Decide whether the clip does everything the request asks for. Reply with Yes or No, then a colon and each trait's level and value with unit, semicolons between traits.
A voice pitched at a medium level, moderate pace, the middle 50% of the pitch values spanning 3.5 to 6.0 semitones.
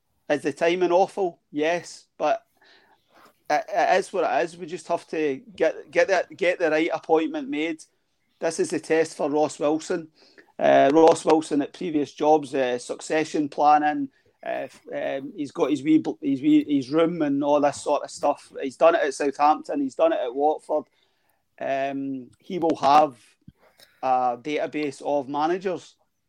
Yes: medium, 160 Hz; average, 170 wpm; average, 3.8 semitones